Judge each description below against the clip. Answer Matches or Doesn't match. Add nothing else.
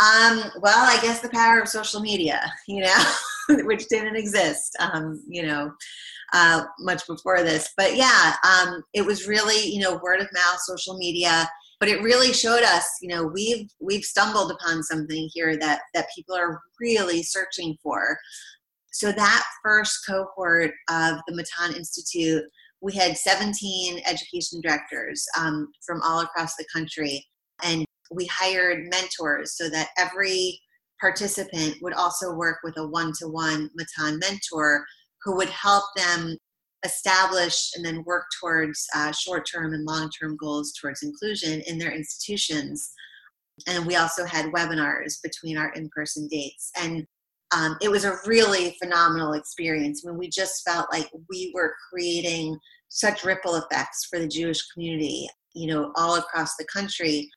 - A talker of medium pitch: Matches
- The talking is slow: Doesn't match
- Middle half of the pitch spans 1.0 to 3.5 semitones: Matches